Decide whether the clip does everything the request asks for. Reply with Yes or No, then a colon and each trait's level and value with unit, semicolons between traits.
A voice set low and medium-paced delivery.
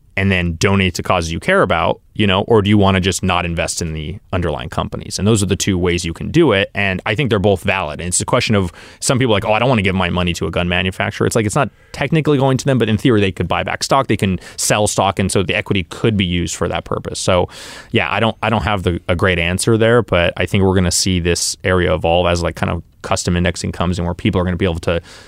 No: very low, 95 Hz; fast, 300 wpm